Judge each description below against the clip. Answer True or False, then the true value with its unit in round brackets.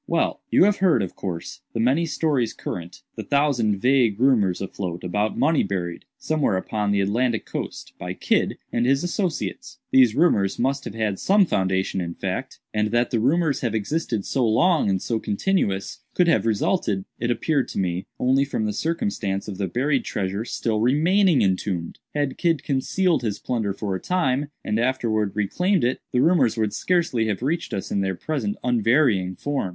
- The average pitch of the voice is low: True (115 Hz)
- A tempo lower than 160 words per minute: False (180 wpm)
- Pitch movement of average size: False (6.8 semitones)